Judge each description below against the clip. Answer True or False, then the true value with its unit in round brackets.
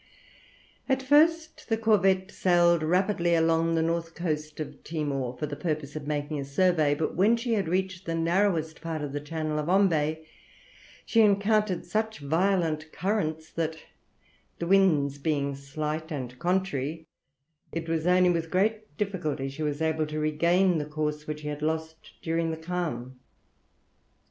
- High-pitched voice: False (160 Hz)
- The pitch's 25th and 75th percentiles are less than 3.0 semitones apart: False (3.5 semitones)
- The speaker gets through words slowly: False (160 wpm)